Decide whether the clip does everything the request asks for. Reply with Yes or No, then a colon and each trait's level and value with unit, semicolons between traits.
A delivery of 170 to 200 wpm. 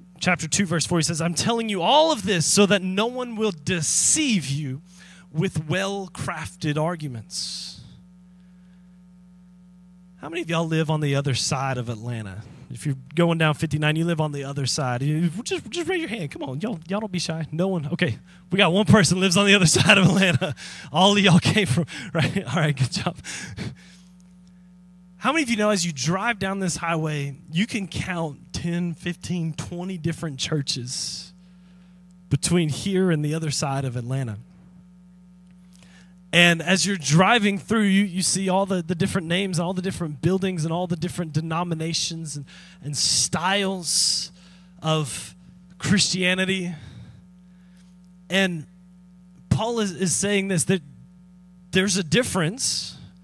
No: average, 160 wpm